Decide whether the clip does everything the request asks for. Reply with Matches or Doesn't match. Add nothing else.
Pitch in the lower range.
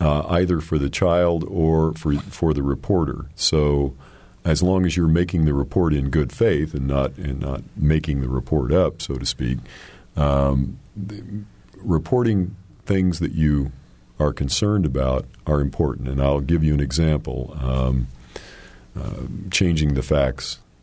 Matches